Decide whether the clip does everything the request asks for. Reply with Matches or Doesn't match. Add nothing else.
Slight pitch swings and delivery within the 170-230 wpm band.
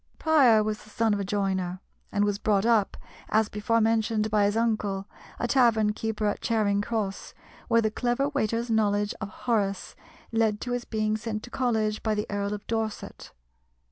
Matches